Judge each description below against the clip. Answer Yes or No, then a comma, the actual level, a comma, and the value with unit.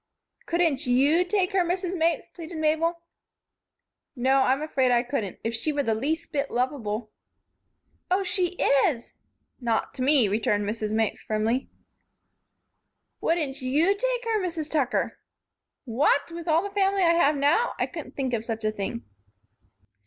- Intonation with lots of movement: Yes, wide, 6.2 semitones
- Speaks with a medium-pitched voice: No, very high, 285 Hz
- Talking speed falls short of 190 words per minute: Yes, average, 160 wpm